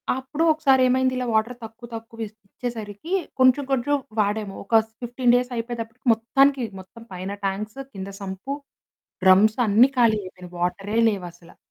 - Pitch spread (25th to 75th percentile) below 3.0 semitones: No, average, 4.1 semitones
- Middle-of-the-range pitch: No, high, 225 Hz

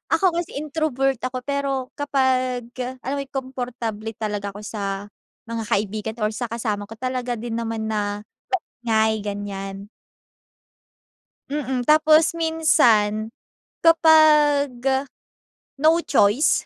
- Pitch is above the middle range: Yes, high, 245 Hz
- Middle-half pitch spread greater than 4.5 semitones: Yes, average, 4.9 semitones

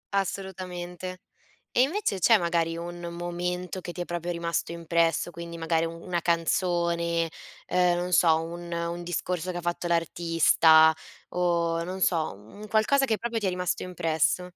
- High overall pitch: No, medium, 175 Hz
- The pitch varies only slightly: Yes, narrow, 1.4 semitones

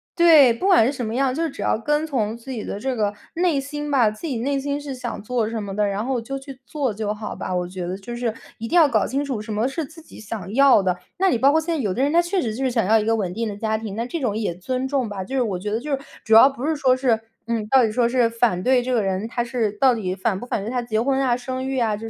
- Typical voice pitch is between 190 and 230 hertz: No, high, 240 Hz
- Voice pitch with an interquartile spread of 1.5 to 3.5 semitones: No, average, 4.0 semitones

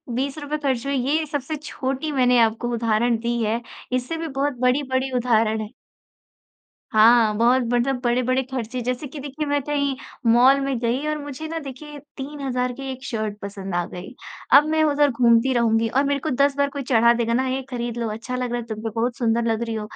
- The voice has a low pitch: No, very high, 255 Hz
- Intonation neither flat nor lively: Yes, average, 3.1 semitones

